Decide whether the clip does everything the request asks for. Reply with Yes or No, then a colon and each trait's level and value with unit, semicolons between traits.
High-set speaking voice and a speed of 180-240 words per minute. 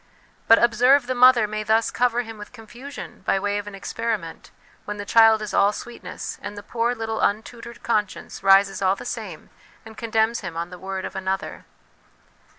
Yes: high, 220 Hz; average, 185 wpm